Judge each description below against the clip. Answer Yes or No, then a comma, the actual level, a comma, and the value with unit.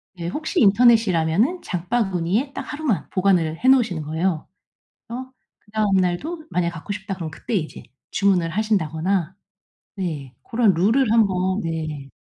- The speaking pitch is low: No, high, 190 Hz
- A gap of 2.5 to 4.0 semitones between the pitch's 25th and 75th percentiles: No, average, 5.2 semitones